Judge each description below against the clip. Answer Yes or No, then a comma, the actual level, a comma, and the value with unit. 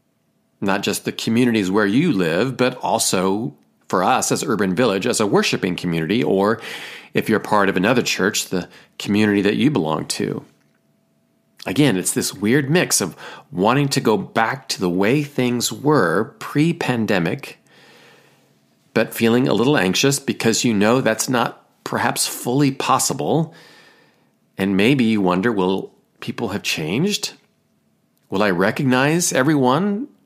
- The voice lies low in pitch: Yes, low, 120 Hz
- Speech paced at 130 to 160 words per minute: Yes, average, 145 wpm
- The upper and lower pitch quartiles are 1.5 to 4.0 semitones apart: No, average, 5.1 semitones